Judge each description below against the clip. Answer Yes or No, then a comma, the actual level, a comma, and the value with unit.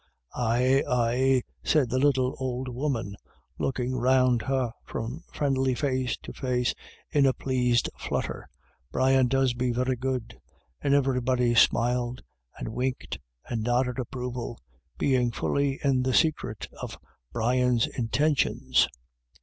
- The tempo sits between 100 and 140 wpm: Yes, slow, 135 wpm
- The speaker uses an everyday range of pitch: No, narrow, 1.5 semitones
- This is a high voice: No, low, 125 Hz